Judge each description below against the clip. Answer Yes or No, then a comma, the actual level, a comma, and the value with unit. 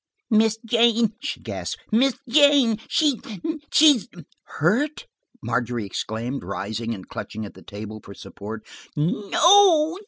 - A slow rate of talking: Yes, slow, 115 wpm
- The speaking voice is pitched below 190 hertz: No, high, 220 Hz